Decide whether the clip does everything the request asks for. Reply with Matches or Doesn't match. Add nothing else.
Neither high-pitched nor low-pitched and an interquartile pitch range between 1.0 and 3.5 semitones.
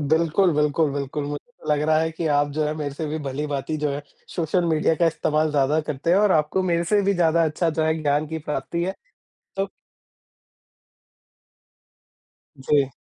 Matches